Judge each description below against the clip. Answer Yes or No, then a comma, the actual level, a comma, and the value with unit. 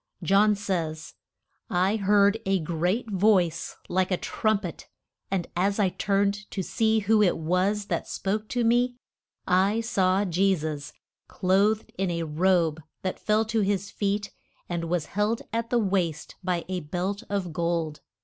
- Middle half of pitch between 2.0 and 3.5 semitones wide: Yes, average, 2.9 semitones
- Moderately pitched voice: No, high, 195 Hz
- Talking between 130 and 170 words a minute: Yes, average, 160 wpm